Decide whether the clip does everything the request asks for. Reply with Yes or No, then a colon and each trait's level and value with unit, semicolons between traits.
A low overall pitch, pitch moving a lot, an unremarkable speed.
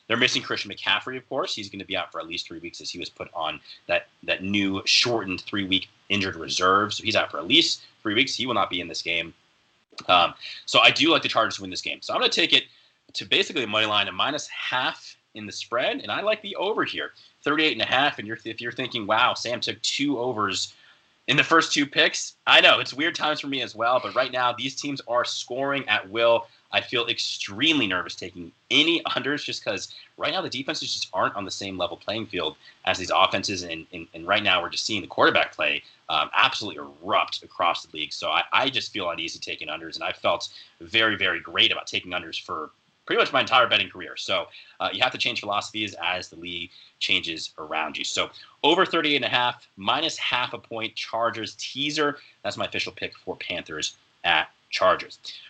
No: low, 115 Hz; wide, 6.6 semitones; fast, 230 wpm